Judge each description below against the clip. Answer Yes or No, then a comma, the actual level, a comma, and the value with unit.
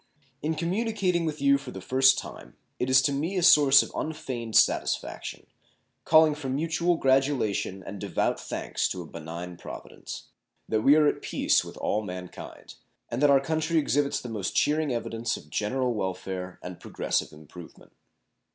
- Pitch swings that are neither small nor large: No, wide, 7.1 semitones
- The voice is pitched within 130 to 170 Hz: Yes, low, 135 Hz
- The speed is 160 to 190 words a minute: Yes, average, 170 wpm